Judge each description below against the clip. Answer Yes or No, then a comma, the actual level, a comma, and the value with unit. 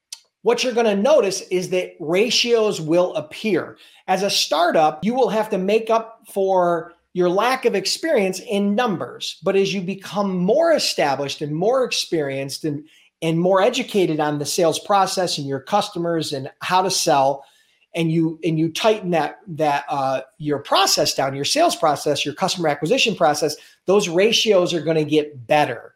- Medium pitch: Yes, medium, 180 Hz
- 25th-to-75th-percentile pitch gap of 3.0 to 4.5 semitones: No, average, 4.9 semitones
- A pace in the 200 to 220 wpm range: No, average, 175 wpm